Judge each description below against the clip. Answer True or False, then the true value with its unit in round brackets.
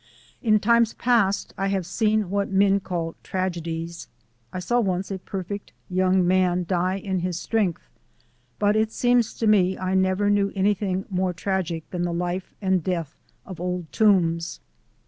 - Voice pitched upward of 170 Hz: True (190 Hz)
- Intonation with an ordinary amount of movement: False (2.3 semitones)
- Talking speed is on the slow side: False (160 wpm)